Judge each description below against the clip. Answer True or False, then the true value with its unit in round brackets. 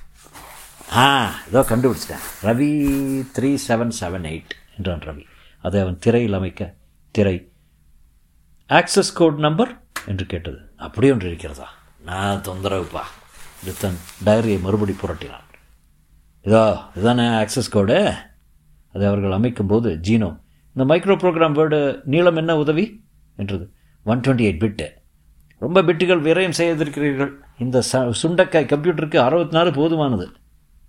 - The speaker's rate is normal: True (115 wpm)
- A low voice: True (110 Hz)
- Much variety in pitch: True (8.3 semitones)